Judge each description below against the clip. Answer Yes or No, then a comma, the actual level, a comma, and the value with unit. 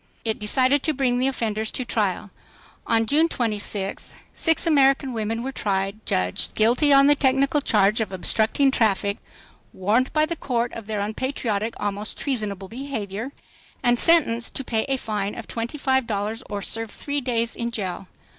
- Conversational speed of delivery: Yes, average, 170 wpm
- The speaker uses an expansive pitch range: No, average, 4.3 semitones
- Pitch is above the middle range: Yes, high, 230 Hz